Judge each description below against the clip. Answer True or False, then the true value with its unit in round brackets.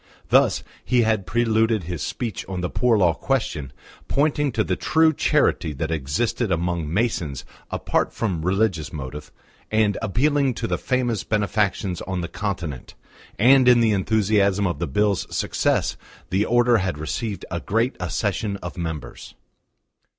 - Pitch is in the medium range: False (100 Hz)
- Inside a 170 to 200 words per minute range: False (150 wpm)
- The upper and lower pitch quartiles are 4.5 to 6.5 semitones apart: True (5.1 semitones)